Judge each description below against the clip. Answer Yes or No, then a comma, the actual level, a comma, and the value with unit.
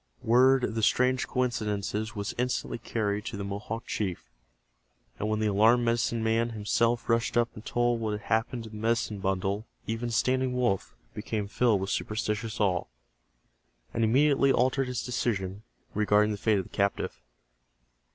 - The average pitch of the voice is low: Yes, low, 110 Hz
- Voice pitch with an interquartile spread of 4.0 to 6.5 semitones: No, narrow, 2.4 semitones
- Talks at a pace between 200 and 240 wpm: No, average, 160 wpm